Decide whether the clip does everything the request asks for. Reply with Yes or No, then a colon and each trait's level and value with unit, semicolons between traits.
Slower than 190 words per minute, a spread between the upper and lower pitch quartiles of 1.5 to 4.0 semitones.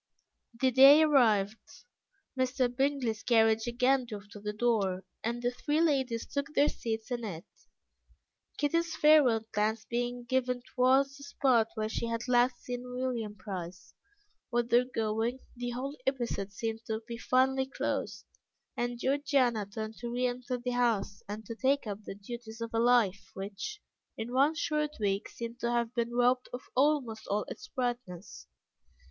Yes: average, 160 wpm; average, 2.7 semitones